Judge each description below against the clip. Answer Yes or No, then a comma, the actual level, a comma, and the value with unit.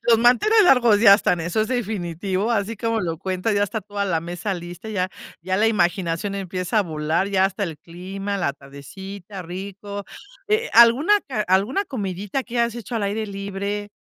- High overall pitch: Yes, high, 200 Hz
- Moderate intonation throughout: Yes, average, 3.4 semitones